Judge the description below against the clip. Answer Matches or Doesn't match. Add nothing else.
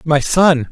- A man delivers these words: Matches